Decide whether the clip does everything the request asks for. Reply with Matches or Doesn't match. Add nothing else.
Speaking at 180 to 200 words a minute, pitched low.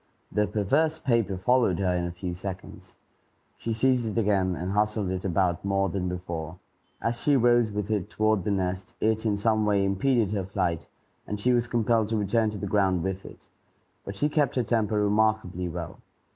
Matches